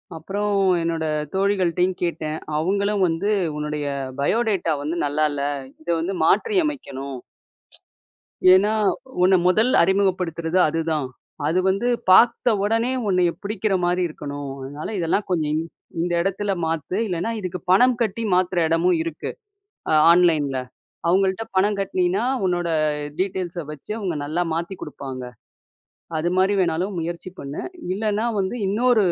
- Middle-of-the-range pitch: Yes, medium, 180 Hz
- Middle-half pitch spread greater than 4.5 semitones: No, average, 3.6 semitones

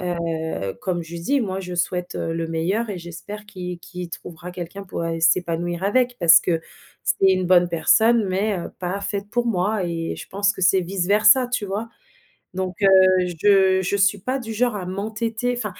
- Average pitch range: Yes, average, 3.1 semitones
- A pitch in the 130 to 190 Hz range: Yes, medium, 185 Hz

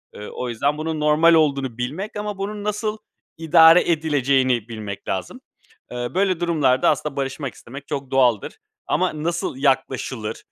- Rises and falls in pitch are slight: No, average, 4.6 semitones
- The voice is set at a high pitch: No, medium, 145 Hz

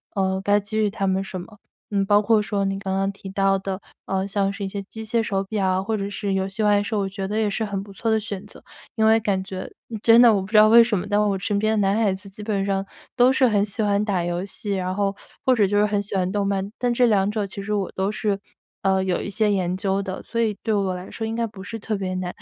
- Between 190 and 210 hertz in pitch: Yes, high, 200 Hz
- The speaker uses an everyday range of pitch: No, narrow, 1.7 semitones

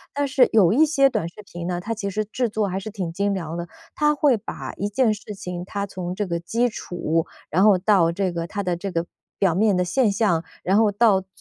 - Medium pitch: No, high, 200 Hz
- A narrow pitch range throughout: No, average, 3.6 semitones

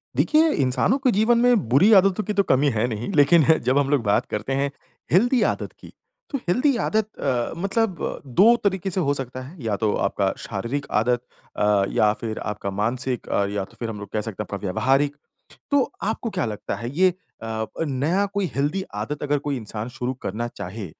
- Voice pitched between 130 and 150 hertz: Yes, low, 135 Hz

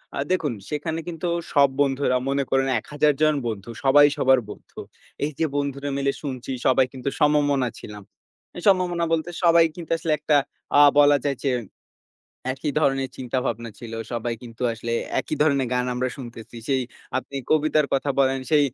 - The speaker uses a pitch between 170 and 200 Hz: No, medium, 140 Hz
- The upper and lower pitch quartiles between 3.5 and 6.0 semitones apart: No, average, 2.8 semitones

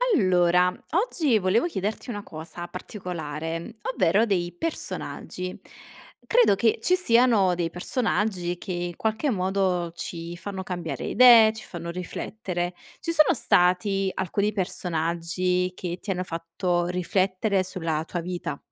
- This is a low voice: No, medium, 185 Hz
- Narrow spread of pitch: No, average, 3.4 semitones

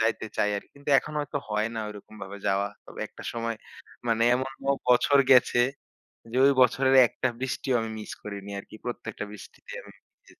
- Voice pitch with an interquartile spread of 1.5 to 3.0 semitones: No, average, 3.8 semitones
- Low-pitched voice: Yes, low, 115 Hz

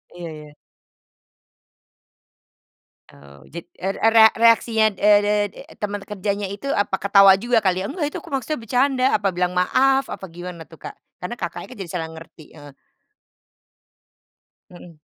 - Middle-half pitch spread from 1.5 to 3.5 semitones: No, average, 4.3 semitones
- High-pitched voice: Yes, high, 200 Hz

